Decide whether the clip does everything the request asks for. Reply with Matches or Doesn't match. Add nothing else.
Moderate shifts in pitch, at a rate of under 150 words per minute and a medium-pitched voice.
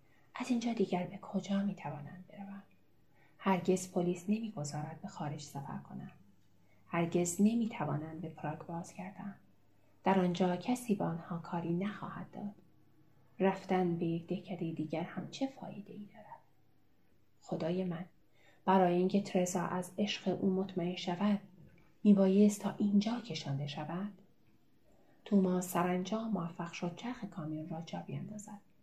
Matches